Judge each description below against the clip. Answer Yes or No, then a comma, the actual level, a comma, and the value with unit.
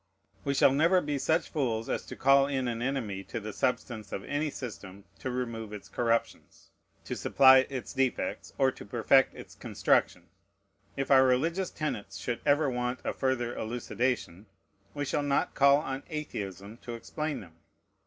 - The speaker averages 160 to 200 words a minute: Yes, average, 165 wpm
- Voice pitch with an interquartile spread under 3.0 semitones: No, average, 3.6 semitones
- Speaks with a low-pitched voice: Yes, low, 130 Hz